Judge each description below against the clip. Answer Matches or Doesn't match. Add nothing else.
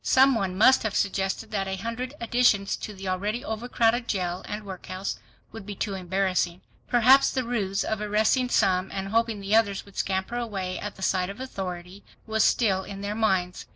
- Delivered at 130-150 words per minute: Doesn't match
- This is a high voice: Matches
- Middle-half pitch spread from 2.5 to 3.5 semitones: Matches